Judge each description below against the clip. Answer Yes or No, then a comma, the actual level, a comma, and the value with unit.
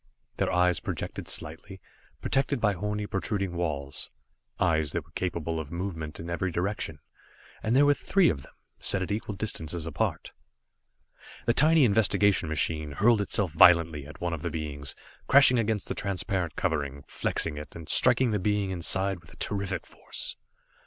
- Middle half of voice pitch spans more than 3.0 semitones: Yes, average, 4.5 semitones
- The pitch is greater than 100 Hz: No, very low, 90 Hz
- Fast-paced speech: No, average, 160 wpm